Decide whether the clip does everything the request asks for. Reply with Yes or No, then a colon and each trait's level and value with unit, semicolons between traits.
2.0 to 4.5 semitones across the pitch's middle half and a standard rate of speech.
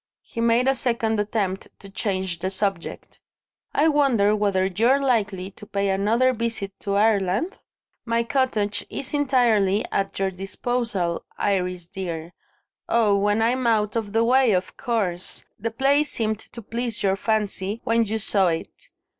Yes: average, 3.2 semitones; average, 155 wpm